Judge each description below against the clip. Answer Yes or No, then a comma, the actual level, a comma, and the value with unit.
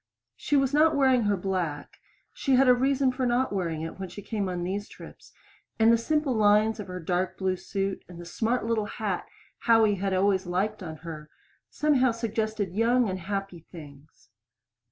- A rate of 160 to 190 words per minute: Yes, average, 185 wpm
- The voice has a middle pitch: No, high, 205 Hz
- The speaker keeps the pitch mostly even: No, average, 4.7 semitones